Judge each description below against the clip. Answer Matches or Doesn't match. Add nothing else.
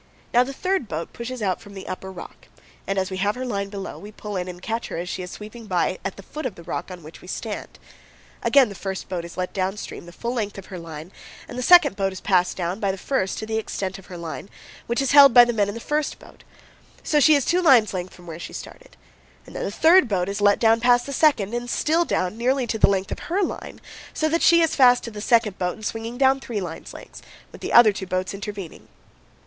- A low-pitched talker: Doesn't match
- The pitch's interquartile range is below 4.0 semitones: Doesn't match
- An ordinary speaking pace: Doesn't match